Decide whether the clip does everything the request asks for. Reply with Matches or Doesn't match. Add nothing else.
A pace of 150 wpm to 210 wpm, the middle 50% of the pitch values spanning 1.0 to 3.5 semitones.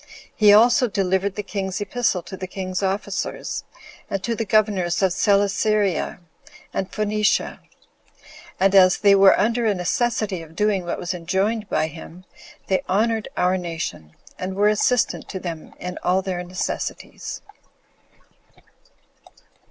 Doesn't match